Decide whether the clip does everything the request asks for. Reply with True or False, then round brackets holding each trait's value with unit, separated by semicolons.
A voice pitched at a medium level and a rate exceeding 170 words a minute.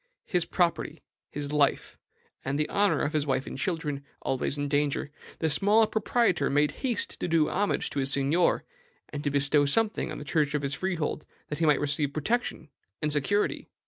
True (150 Hz; 185 wpm)